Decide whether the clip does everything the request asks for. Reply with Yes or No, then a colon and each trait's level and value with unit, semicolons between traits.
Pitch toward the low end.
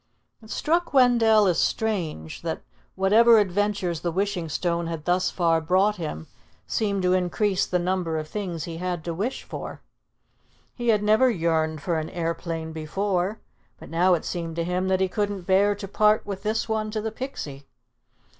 No: medium, 185 Hz